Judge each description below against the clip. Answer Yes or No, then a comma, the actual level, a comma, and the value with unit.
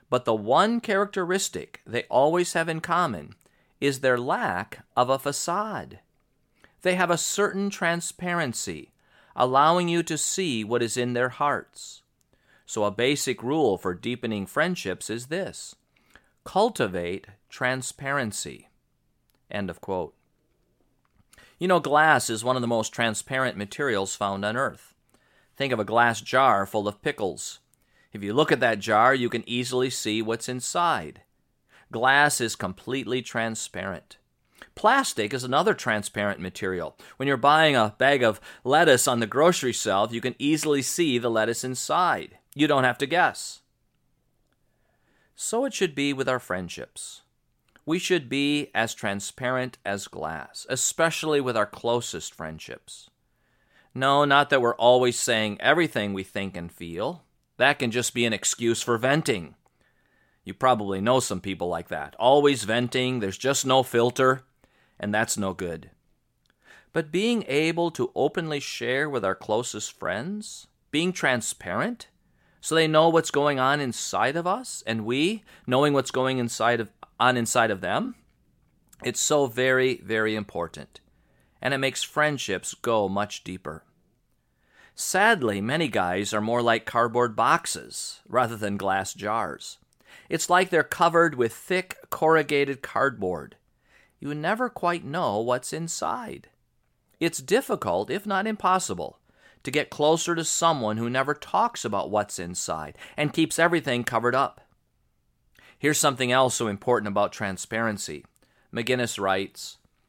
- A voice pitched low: Yes, low, 130 Hz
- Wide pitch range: Yes, wide, 5.7 semitones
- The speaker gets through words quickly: No, average, 140 wpm